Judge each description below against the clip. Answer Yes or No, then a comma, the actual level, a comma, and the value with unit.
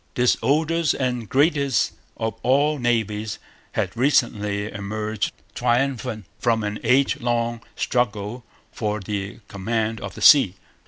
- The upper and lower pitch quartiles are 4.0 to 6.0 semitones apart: No, average, 3.5 semitones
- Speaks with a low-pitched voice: Yes, low, 115 Hz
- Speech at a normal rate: No, slow, 120 wpm